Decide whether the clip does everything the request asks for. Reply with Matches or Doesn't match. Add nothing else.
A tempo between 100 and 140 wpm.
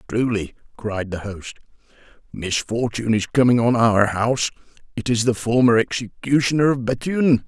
Matches